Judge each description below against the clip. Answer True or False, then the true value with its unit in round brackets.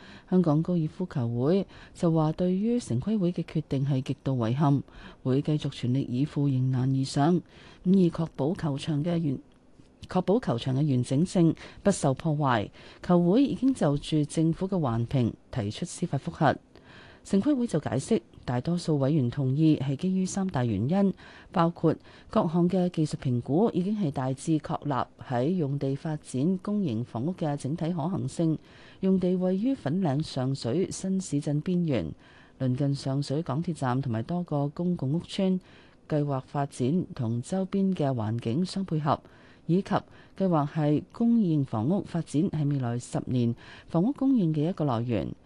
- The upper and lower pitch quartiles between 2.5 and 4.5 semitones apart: False (5.0 semitones)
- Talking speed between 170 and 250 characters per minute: True (245 characters per minute)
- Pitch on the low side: False (155 Hz)